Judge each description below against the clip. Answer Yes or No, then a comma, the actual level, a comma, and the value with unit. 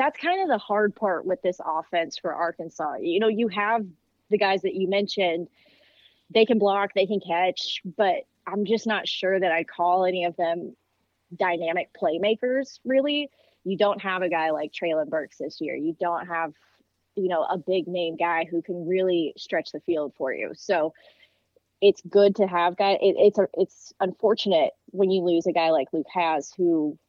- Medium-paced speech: Yes, average, 195 wpm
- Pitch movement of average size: Yes, average, 3.3 semitones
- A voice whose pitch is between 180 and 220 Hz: Yes, medium, 185 Hz